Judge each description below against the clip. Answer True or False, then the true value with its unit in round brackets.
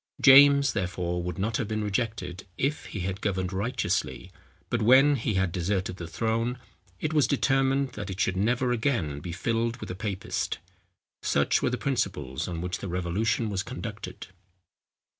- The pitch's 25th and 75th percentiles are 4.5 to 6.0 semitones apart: True (5.2 semitones)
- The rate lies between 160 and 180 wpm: True (165 wpm)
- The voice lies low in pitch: True (105 Hz)